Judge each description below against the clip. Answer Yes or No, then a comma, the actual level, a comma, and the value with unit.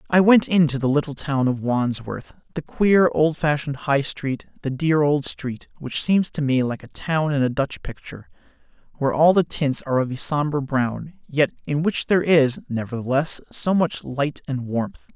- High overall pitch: No, medium, 145 Hz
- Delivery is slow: No, average, 190 wpm